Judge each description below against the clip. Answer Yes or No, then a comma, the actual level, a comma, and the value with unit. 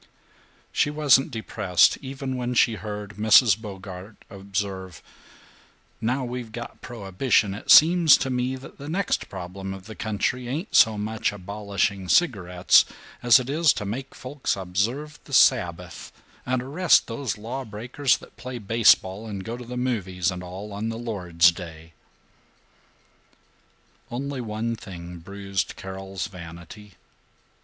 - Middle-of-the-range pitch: No, low, 110 Hz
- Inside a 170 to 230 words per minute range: No, average, 140 wpm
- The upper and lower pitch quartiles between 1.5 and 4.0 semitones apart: No, average, 4.7 semitones